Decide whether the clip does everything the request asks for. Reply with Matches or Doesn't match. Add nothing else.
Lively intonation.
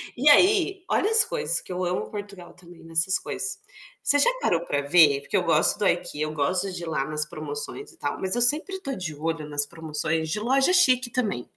Matches